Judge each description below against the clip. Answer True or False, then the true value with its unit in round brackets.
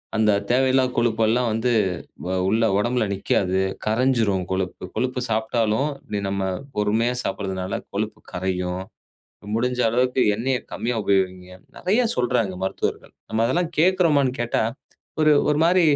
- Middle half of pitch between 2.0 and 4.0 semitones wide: False (4.5 semitones)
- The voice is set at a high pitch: False (115 Hz)